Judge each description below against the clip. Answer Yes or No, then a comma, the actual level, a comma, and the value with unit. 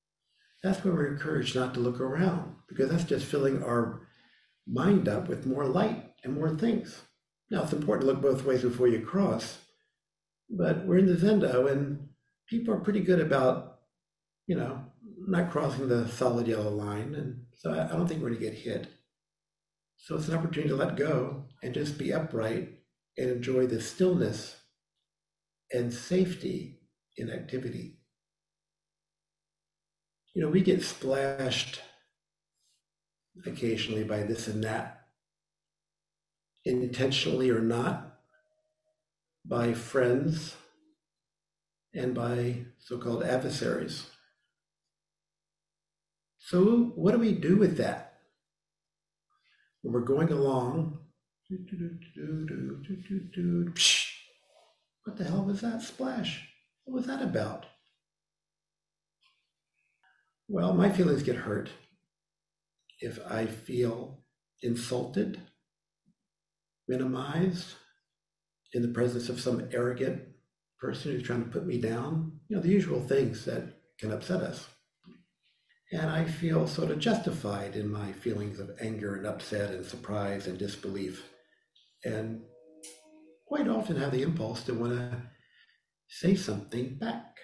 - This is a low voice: No, medium, 155 Hz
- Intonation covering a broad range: Yes, wide, 6.3 semitones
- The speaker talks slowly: Yes, slow, 130 wpm